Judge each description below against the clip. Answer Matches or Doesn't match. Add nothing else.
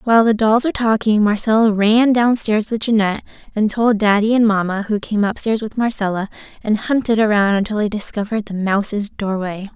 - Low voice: Doesn't match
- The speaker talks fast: Doesn't match